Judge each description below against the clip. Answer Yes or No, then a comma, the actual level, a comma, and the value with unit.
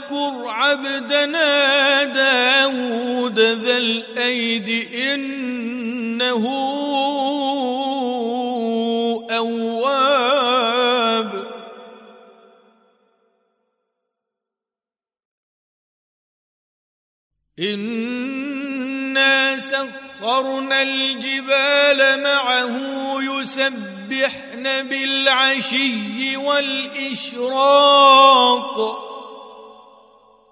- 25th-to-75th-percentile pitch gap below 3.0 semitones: Yes, narrow, 2.6 semitones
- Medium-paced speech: No, slow, 30 wpm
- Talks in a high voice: Yes, very high, 265 Hz